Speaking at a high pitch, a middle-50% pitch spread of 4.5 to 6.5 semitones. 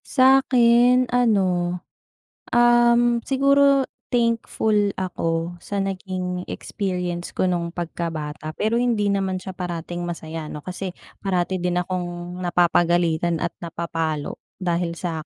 No: medium, 180 Hz; average, 5.0 semitones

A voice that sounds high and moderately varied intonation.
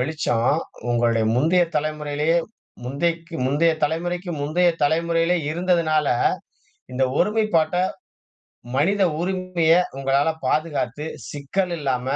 No: medium, 160 Hz; average, 3.4 semitones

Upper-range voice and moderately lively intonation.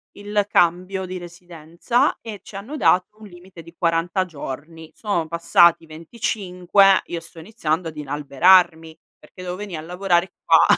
No: medium, 175 Hz; average, 3.0 semitones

